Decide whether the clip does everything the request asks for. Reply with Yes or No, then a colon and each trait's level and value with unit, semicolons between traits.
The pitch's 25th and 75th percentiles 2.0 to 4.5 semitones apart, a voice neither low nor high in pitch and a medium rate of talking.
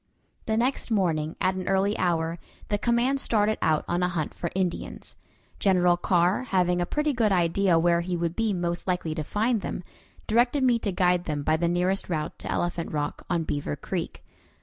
Yes: average, 3.5 semitones; medium, 180 Hz; average, 195 wpm